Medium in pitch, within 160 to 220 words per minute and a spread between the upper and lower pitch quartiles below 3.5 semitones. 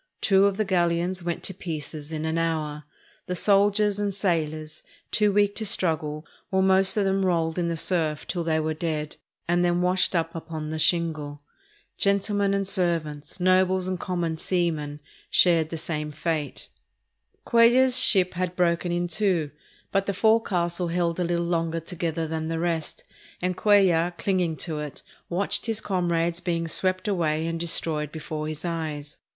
Yes: medium, 170 Hz; average, 165 wpm; average, 2.9 semitones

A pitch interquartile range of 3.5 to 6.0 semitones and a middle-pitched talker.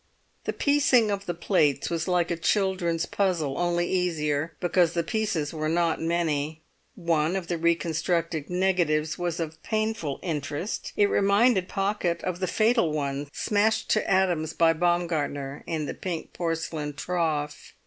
No: average, 3.1 semitones; medium, 170 Hz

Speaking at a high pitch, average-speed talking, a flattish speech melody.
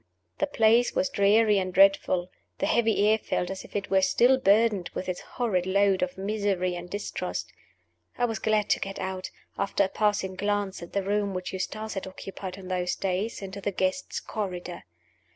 Yes: high, 195 Hz; average, 190 wpm; narrow, 2.2 semitones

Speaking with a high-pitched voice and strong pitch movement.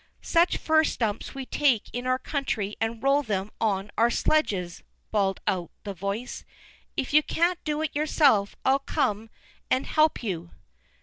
Yes: high, 240 Hz; wide, 6.4 semitones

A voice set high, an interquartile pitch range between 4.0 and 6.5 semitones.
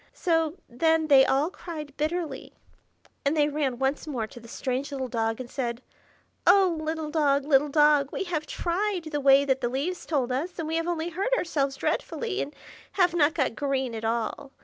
No: very high, 295 Hz; average, 3.6 semitones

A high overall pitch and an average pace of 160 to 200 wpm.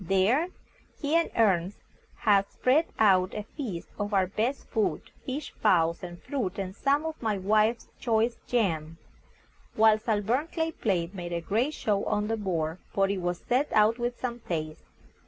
Yes: high, 210 Hz; average, 175 wpm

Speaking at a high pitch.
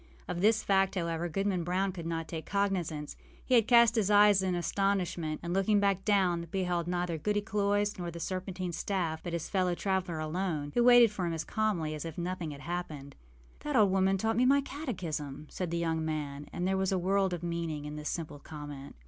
No: medium, 180 Hz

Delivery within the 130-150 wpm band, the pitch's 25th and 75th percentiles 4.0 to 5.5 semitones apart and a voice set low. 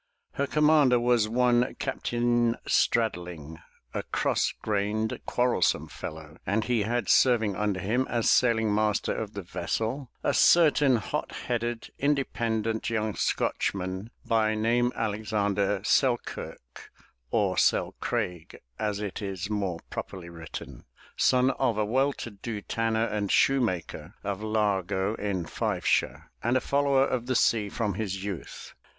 No: slow, 135 wpm; average, 3.3 semitones; low, 110 Hz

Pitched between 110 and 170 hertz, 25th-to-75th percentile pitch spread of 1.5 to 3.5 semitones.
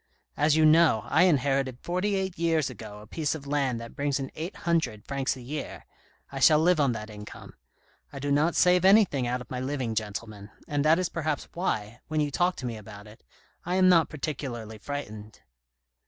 No: medium, 140 Hz; wide, 5.6 semitones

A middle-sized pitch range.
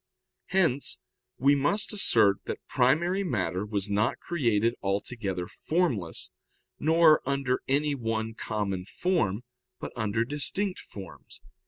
No: wide, 7.1 semitones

